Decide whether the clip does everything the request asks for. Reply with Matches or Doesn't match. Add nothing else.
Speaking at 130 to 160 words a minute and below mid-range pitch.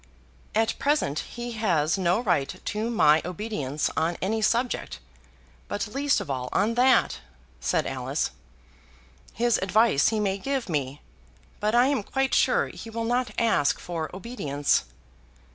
Doesn't match